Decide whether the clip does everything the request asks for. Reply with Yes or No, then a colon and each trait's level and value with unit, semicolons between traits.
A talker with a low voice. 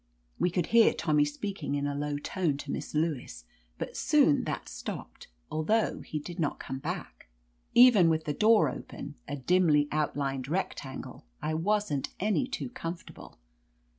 No: medium, 155 Hz